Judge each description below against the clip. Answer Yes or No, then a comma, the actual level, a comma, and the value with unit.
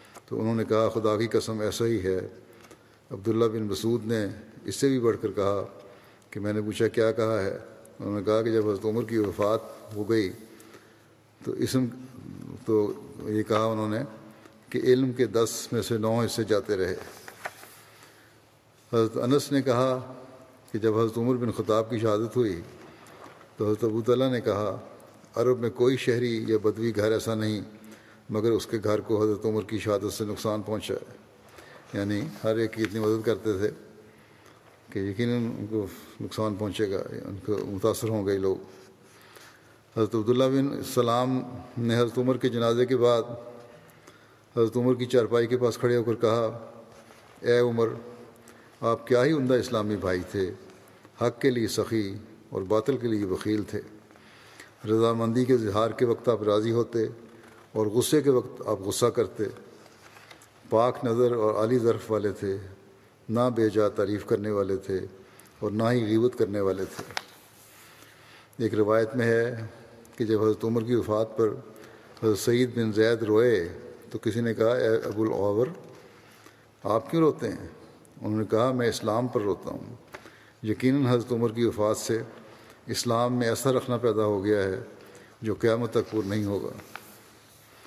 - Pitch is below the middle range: Yes, low, 115 Hz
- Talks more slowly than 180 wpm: Yes, average, 170 wpm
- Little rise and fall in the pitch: Yes, narrow, 1.9 semitones